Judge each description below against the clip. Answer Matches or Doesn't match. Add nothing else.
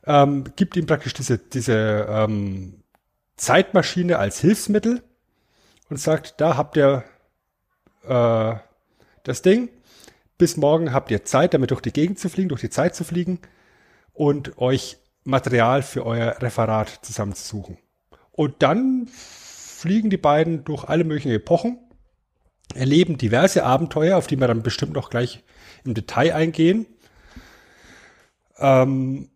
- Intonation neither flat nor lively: Doesn't match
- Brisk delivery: Doesn't match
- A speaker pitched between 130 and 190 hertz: Matches